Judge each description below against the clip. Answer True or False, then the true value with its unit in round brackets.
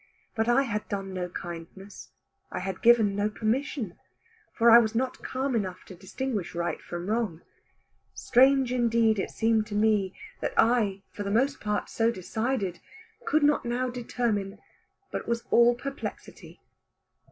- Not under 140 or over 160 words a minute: True (150 wpm)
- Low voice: False (225 Hz)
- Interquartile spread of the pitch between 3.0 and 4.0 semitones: True (3.5 semitones)